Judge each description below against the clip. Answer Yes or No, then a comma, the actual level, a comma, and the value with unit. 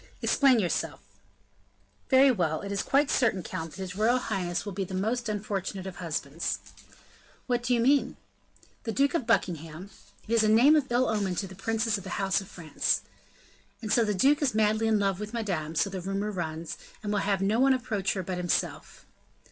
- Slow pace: No, fast, 205 wpm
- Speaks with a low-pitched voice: No, high, 205 Hz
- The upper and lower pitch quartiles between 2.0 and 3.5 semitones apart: No, average, 3.9 semitones